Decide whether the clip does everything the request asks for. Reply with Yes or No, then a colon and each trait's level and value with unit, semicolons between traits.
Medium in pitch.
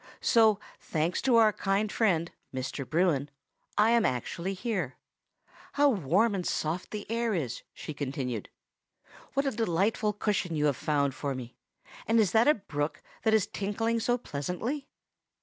No: high, 195 Hz